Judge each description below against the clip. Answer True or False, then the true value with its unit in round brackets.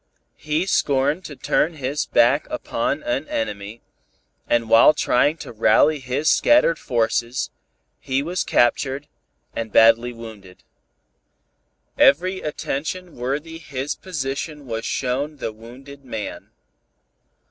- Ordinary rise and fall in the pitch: True (4.4 semitones)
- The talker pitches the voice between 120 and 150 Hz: True (135 Hz)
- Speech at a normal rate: False (110 wpm)